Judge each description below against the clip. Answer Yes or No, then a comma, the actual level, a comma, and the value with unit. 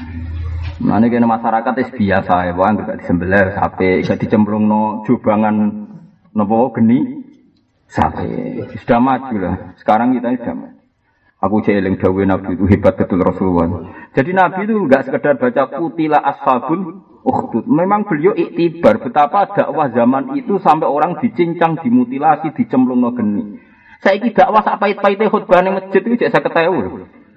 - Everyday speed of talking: Yes, average, 130 wpm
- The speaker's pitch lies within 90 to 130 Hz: No, medium, 170 Hz